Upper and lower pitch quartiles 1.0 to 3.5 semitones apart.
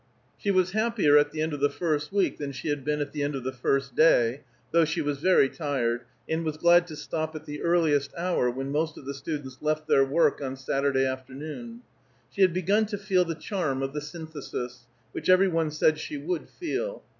No: average, 4.0 semitones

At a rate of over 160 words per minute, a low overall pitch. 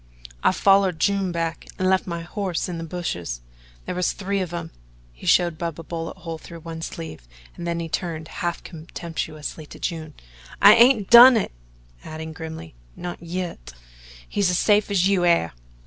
No: average, 180 wpm; medium, 170 Hz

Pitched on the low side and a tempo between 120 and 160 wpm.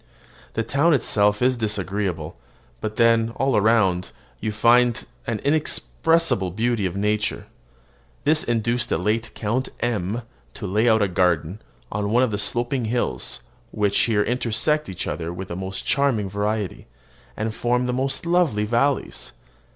Yes: low, 110 Hz; average, 150 wpm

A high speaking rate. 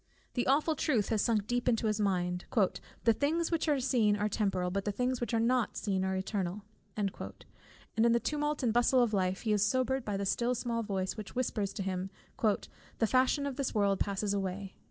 Yes: fast, 210 wpm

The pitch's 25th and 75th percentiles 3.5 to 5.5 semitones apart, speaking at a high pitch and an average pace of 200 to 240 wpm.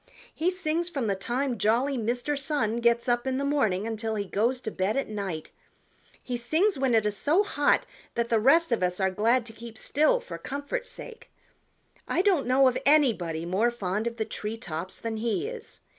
Yes: average, 4.9 semitones; high, 240 Hz; fast, 205 wpm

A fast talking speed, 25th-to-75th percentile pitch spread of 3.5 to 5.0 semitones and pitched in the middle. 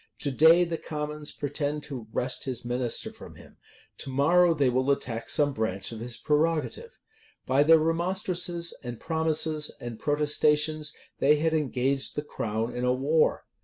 No: average, 160 wpm; average, 3.9 semitones; medium, 150 Hz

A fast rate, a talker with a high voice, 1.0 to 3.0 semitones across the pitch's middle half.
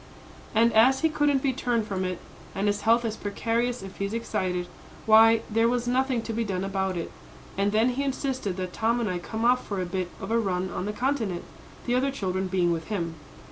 No: fast, 225 wpm; high, 220 Hz; average, 4.3 semitones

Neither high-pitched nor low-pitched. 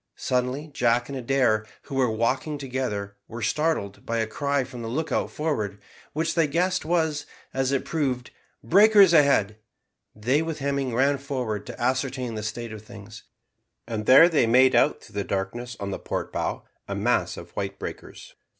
No: low, 130 Hz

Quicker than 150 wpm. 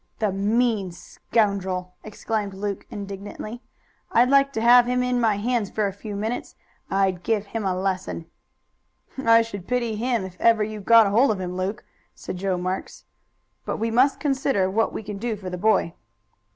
Yes: average, 180 wpm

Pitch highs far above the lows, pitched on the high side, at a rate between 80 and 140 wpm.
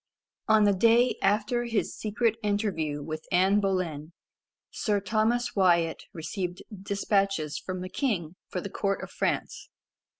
No: average, 3.4 semitones; high, 195 Hz; slow, 135 wpm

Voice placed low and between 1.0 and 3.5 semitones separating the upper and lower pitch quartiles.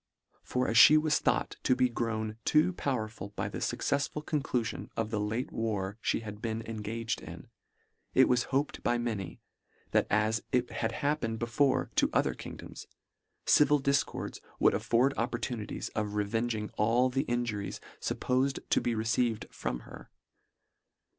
Yes: low, 115 Hz; average, 2.8 semitones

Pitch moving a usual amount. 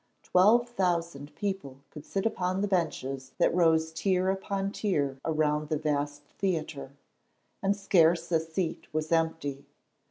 Yes: average, 4.3 semitones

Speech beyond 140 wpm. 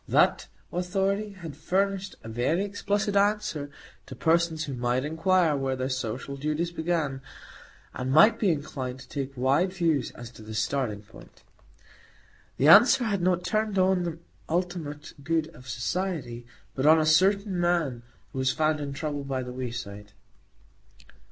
Yes: average, 155 wpm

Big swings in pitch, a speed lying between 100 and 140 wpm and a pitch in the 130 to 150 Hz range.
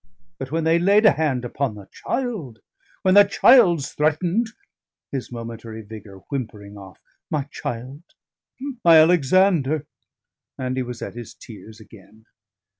Yes: wide, 6.8 semitones; slow, 135 wpm; low, 135 Hz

